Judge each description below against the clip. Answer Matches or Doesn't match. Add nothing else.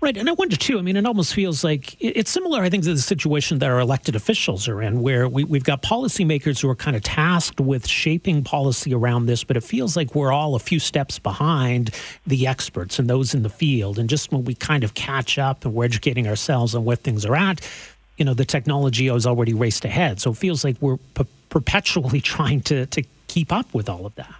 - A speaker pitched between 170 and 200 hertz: Doesn't match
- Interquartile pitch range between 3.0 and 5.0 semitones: Matches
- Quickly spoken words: Matches